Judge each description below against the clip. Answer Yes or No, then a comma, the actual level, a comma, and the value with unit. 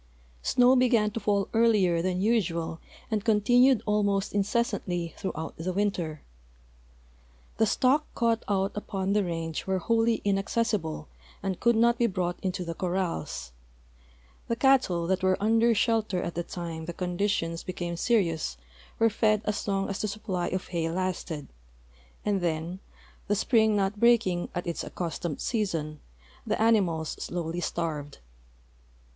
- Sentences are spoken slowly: No, average, 145 wpm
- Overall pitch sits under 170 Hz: No, high, 195 Hz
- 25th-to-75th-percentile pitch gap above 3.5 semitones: Yes, average, 4.2 semitones